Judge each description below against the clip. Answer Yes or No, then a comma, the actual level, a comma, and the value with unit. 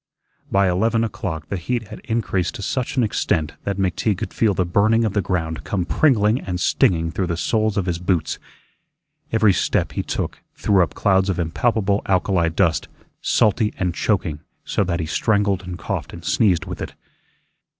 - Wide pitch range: No, average, 3.4 semitones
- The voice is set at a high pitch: No, very low, 95 Hz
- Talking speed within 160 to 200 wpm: Yes, average, 180 wpm